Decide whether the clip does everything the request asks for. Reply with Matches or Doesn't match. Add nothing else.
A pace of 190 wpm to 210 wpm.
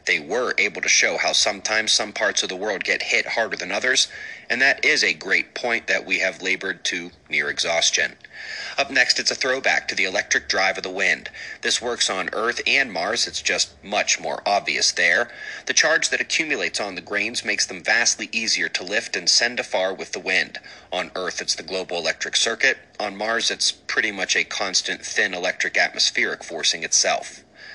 Matches